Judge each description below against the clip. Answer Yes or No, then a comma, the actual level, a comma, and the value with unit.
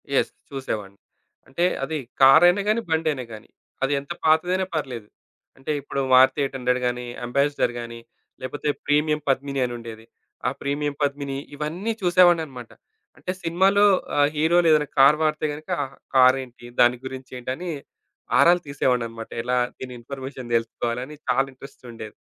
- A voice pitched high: No, low, 135 Hz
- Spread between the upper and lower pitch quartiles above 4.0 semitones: No, average, 3.6 semitones